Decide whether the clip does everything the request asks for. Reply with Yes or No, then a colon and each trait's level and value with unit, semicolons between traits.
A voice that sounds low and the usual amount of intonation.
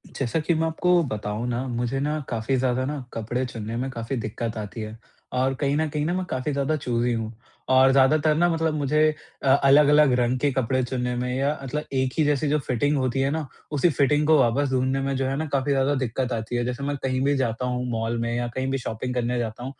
Yes: low, 130 Hz; average, 3.1 semitones